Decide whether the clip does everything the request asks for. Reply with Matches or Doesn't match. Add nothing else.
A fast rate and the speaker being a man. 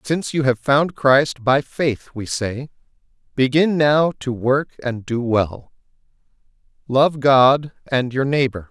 Doesn't match